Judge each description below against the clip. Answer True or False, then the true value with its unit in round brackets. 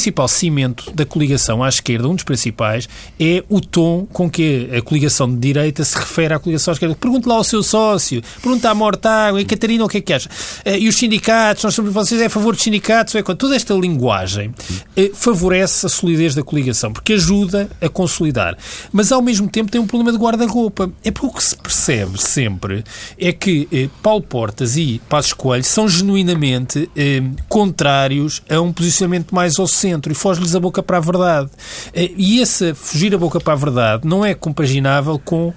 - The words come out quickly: True (190 wpm)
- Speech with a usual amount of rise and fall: False (7.0 semitones)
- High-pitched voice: False (175 Hz)